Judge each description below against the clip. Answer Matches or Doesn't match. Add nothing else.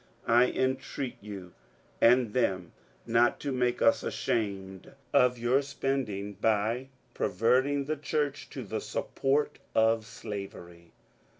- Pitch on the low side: Matches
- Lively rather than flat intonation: Doesn't match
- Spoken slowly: Matches